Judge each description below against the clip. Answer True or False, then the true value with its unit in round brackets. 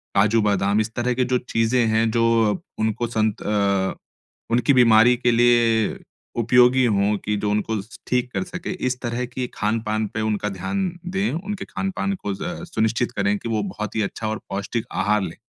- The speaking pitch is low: True (115 Hz)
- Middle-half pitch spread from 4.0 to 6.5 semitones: False (2.7 semitones)